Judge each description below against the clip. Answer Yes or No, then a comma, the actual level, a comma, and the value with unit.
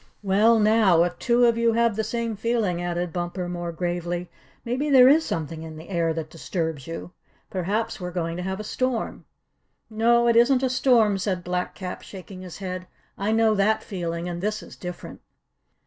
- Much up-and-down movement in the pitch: No, average, 4.6 semitones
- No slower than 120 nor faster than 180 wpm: No, average, 190 wpm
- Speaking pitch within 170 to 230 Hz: Yes, high, 190 Hz